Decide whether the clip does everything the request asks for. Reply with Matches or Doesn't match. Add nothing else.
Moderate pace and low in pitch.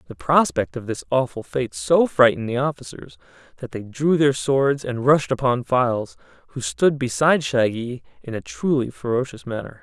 Matches